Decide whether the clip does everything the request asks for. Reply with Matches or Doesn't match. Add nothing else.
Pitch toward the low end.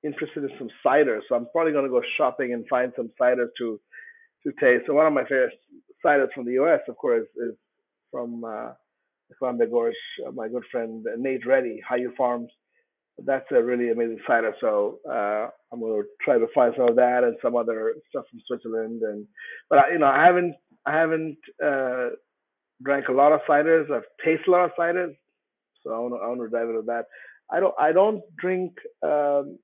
Doesn't match